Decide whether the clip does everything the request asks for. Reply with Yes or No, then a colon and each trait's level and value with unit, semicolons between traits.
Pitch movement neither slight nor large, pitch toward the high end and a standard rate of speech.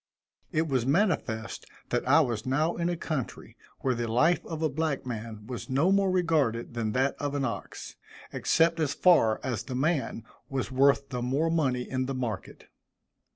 No: average, 4.6 semitones; low, 135 Hz; average, 180 wpm